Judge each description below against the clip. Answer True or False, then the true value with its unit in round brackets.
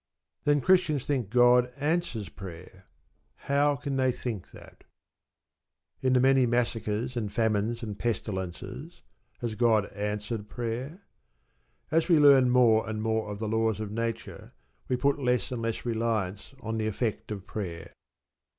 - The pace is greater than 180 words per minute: False (145 wpm)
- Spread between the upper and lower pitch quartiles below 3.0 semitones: False (3.3 semitones)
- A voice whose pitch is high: False (115 Hz)